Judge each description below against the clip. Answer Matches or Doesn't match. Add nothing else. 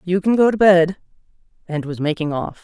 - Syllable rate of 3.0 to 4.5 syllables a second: Doesn't match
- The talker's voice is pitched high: Doesn't match